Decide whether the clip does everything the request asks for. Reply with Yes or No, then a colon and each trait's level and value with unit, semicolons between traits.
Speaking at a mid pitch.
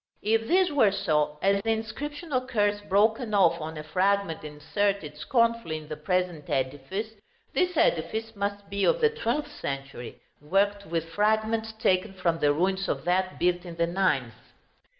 No: high, 195 Hz